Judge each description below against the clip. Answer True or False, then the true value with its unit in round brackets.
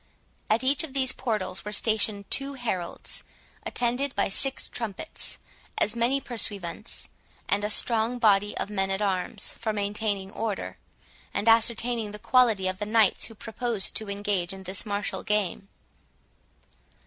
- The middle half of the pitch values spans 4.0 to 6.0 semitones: False (2.8 semitones)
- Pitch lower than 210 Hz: False (215 Hz)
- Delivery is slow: False (150 wpm)